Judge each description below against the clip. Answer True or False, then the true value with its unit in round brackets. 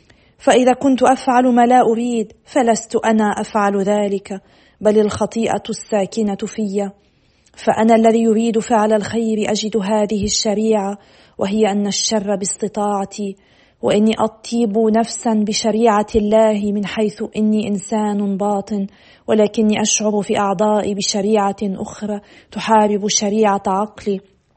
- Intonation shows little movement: True (1.4 semitones)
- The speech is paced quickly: False (110 wpm)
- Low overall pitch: False (215 Hz)